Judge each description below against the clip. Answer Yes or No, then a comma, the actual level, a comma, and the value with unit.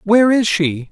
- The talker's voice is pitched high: Yes, high, 200 Hz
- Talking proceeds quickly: No, average, 195 wpm